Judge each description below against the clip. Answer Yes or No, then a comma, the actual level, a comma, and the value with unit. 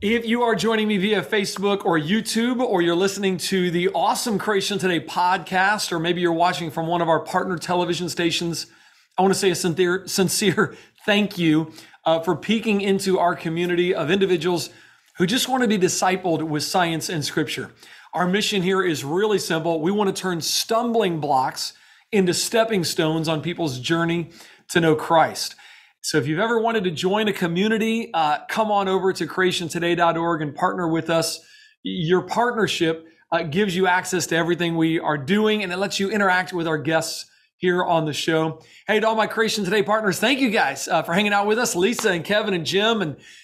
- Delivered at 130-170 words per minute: No, average, 195 wpm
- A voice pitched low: No, medium, 180 Hz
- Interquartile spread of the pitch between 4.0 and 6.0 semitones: No, average, 3.6 semitones